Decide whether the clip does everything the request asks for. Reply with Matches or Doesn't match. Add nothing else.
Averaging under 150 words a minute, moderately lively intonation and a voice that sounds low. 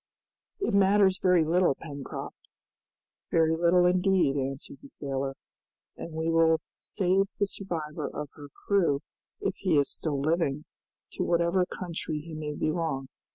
Doesn't match